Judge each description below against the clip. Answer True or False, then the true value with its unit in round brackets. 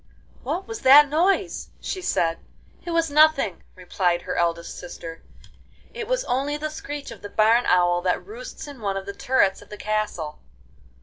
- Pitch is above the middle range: True (245 Hz)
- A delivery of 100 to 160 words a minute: False (175 wpm)